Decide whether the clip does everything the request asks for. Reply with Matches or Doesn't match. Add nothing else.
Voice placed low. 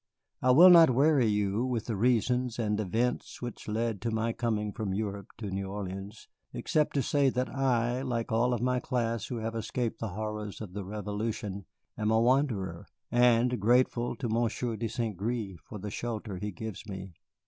Matches